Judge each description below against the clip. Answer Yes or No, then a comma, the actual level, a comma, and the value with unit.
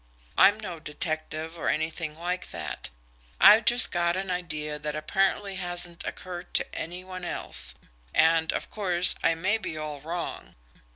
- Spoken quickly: No, average, 155 wpm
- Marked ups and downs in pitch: No, average, 2.7 semitones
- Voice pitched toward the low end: No, medium, 175 Hz